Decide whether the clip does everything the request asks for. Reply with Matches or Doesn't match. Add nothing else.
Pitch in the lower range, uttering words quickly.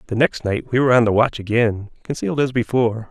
Matches